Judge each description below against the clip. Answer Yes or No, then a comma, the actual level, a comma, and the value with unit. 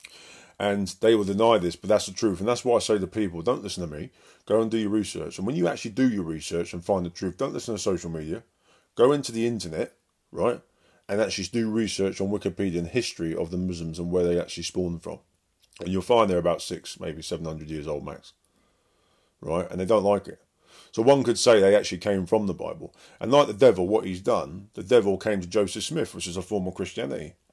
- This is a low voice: Yes, very low, 95 Hz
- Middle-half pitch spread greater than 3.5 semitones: Yes, average, 3.9 semitones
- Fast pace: Yes, fast, 240 wpm